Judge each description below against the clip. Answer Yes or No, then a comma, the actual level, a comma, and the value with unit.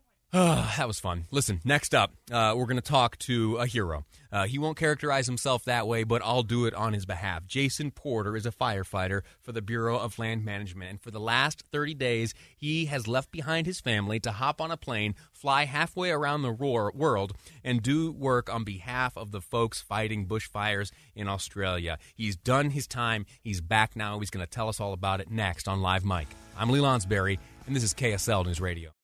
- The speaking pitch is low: Yes, low, 115 Hz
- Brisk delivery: Yes, fast, 215 wpm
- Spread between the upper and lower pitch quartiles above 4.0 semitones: Yes, average, 4.6 semitones